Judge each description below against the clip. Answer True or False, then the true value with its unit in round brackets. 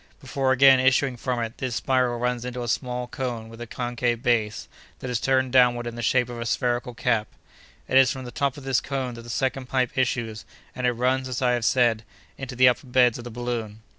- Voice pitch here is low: True (125 Hz)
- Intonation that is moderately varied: False (1.5 semitones)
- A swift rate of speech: True (230 wpm)